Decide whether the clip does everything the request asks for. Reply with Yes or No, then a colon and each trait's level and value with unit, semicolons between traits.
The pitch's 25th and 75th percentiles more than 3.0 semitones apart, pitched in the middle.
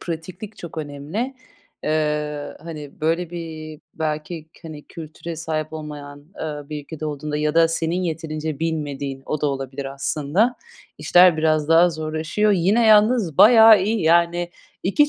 No: narrow, 2.5 semitones; medium, 160 Hz